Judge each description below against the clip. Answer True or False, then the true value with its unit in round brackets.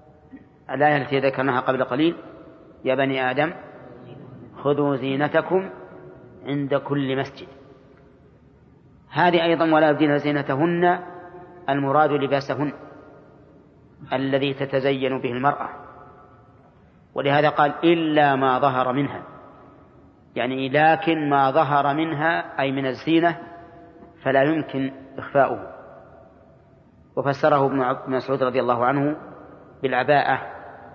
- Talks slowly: False (95 wpm)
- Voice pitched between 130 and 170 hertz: True (140 Hz)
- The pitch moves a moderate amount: False (2.3 semitones)